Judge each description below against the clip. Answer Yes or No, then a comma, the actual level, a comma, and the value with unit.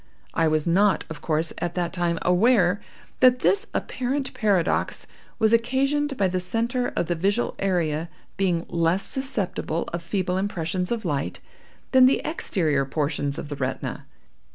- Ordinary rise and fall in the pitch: No, wide, 5.9 semitones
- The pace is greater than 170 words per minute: No, average, 155 wpm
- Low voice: No, medium, 185 Hz